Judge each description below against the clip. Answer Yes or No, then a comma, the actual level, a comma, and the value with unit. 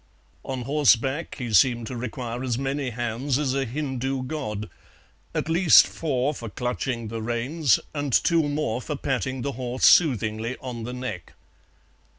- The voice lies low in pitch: Yes, low, 130 Hz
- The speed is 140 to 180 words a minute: Yes, average, 155 wpm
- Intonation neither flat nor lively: Yes, average, 3.1 semitones